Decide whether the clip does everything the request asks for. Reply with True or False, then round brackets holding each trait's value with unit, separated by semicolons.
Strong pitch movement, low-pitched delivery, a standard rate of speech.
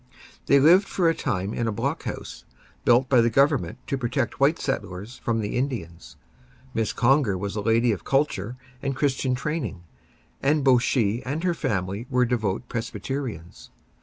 False (4.7 semitones; 125 Hz; 165 wpm)